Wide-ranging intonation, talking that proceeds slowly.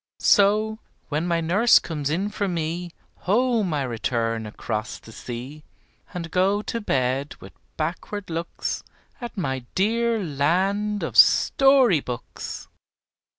Yes: wide, 6.6 semitones; slow, 125 wpm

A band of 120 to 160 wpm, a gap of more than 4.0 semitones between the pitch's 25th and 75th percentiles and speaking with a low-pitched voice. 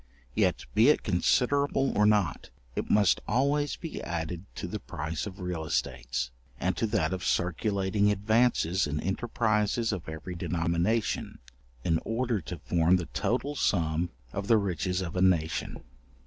Yes: average, 150 wpm; average, 4.7 semitones; very low, 95 Hz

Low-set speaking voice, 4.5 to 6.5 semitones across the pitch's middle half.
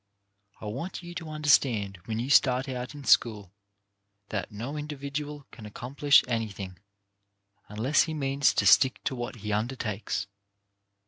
Yes: low, 125 Hz; average, 5.1 semitones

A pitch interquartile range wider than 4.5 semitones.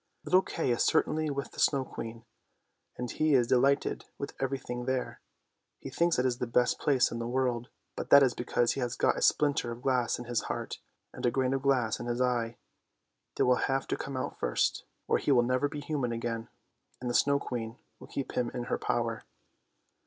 No: narrow, 2.4 semitones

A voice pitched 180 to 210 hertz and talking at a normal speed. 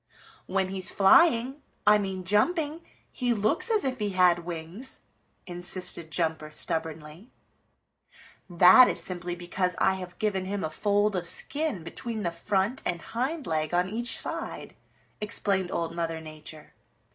Yes: high, 190 Hz; average, 145 wpm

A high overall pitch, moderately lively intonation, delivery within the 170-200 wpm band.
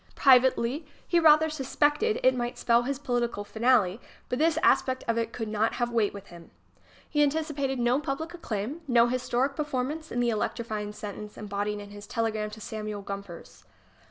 Yes: high, 240 Hz; average, 4.7 semitones; average, 175 wpm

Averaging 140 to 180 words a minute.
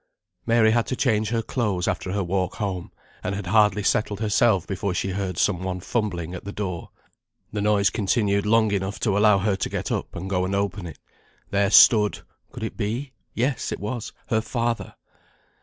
No: average, 190 wpm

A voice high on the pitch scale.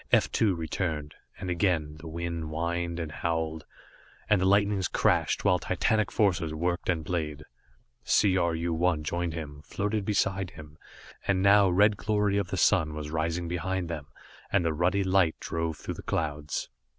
No: very low, 85 Hz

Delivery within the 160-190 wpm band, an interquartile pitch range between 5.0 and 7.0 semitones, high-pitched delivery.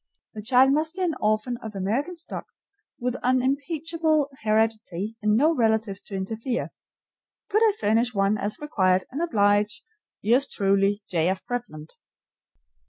No: average, 140 wpm; wide, 5.4 semitones; high, 225 Hz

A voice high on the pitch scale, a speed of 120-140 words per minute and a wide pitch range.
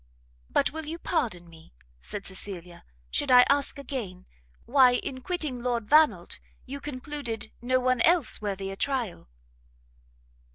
Yes: very high, 250 Hz; slow, 135 wpm; wide, 5.9 semitones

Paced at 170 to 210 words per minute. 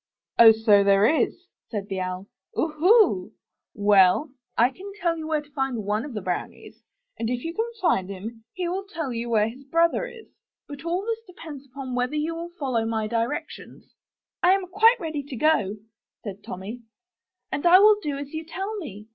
Yes: average, 190 wpm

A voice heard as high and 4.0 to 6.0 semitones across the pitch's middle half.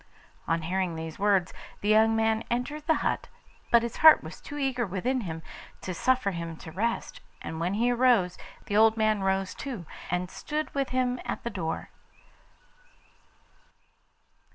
Yes: high, 215 Hz; wide, 5.4 semitones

